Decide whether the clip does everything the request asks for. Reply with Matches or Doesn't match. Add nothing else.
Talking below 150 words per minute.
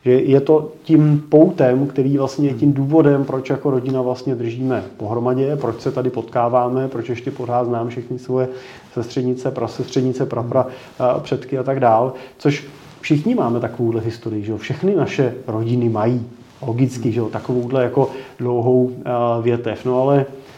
Doesn't match